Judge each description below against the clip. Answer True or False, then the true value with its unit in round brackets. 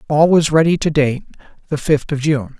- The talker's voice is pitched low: False (150 Hz)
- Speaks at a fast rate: True (210 wpm)